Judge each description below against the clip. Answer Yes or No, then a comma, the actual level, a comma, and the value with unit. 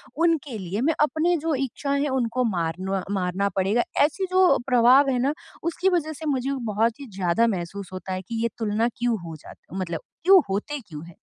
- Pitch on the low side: No, high, 235 Hz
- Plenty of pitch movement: Yes, wide, 7.3 semitones